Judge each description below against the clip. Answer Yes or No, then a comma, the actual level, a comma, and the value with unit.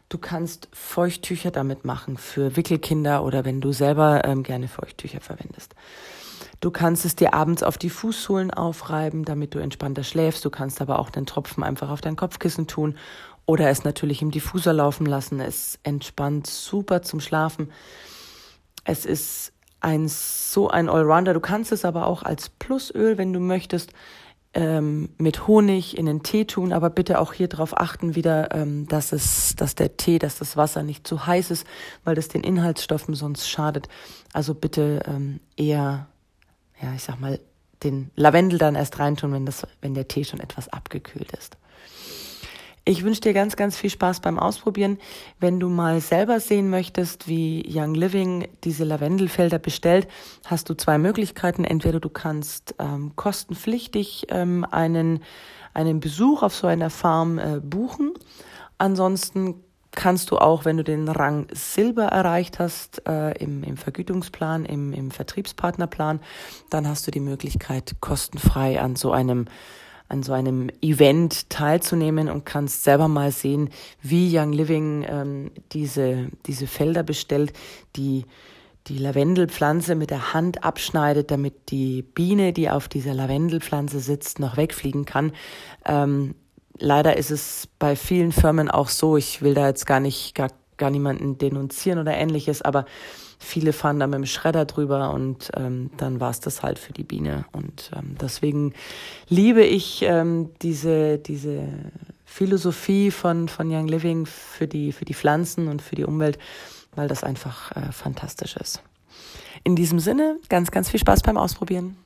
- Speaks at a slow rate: No, average, 160 wpm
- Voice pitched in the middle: Yes, medium, 155 Hz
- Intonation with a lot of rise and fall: No, average, 3.5 semitones